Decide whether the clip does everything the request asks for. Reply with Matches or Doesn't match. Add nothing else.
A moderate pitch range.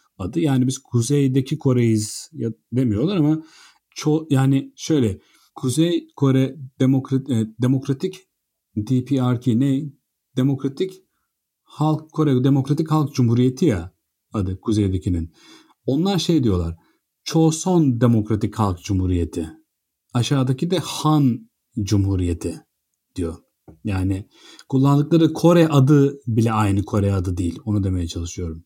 Doesn't match